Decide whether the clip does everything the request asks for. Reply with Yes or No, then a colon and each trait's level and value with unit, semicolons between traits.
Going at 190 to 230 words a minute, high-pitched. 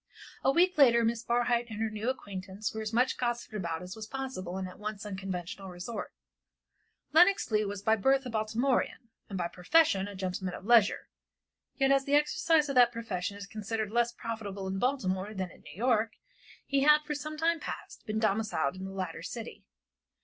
Yes: average, 195 wpm; high, 220 Hz